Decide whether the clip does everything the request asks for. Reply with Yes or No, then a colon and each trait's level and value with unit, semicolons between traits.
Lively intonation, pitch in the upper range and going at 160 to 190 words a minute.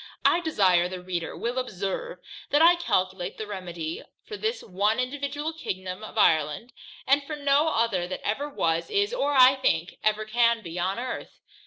Yes: wide, 7.8 semitones; high, 225 Hz; average, 175 wpm